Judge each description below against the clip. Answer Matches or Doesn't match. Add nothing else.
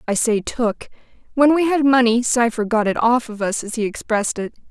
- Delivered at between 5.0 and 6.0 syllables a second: Matches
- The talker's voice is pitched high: Matches